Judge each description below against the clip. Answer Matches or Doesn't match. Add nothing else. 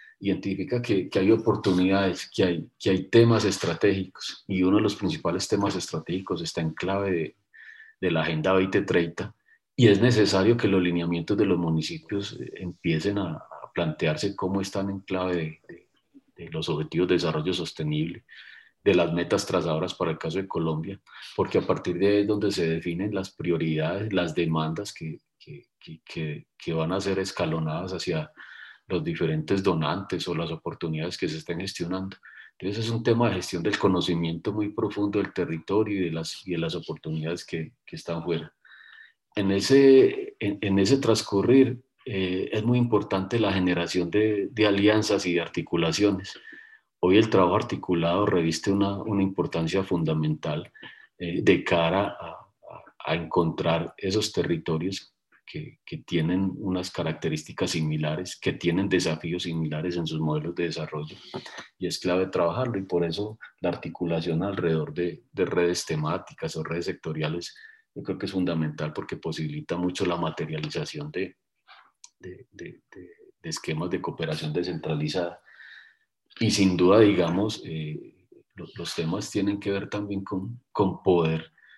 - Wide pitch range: Doesn't match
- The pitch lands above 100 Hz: Doesn't match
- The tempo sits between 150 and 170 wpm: Matches